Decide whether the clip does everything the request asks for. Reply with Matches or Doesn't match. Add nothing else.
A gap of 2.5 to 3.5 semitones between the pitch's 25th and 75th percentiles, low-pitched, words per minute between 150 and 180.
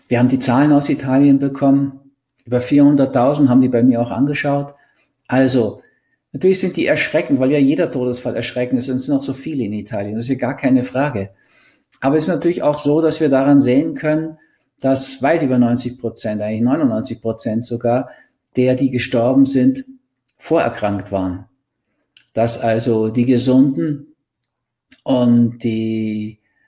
Matches